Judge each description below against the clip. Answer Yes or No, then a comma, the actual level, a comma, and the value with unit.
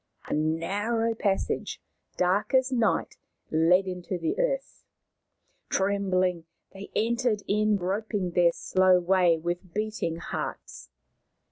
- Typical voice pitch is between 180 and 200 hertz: Yes, high, 190 Hz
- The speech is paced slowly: Yes, slow, 110 wpm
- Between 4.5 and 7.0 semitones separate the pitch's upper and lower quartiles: No, average, 3.3 semitones